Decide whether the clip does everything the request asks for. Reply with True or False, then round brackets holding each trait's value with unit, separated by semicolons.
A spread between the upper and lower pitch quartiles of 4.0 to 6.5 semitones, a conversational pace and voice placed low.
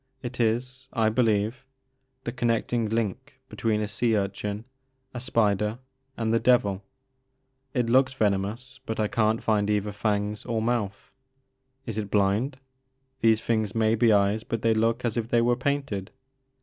False (2.4 semitones; 155 wpm; 110 Hz)